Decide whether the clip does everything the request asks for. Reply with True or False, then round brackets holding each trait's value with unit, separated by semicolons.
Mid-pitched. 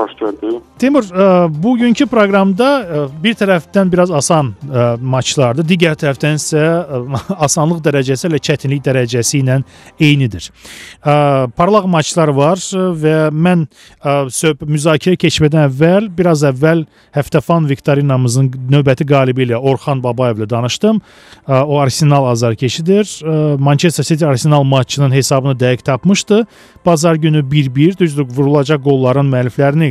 True (150 Hz)